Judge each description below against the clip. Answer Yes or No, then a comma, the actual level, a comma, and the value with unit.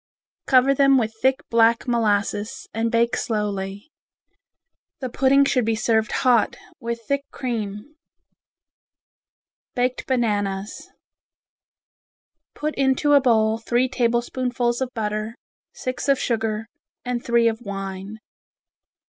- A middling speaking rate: No, slow, 110 wpm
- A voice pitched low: No, high, 235 Hz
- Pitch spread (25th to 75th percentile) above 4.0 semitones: No, average, 2.9 semitones